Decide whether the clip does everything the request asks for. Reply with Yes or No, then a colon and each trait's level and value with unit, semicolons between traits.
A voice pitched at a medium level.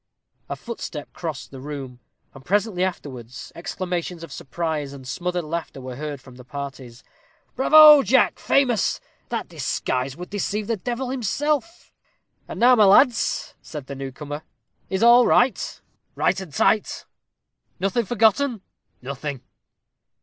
Yes: medium, 175 Hz